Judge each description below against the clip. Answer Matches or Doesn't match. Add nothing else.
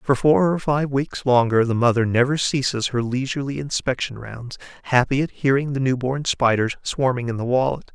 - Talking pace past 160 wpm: Matches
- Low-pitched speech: Matches